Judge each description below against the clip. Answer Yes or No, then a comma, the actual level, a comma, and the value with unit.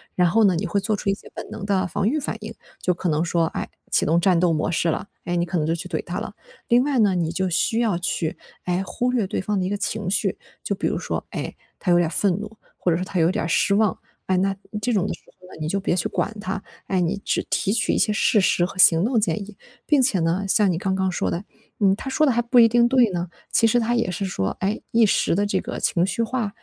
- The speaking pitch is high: Yes, high, 195 Hz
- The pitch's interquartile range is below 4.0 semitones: Yes, average, 3.6 semitones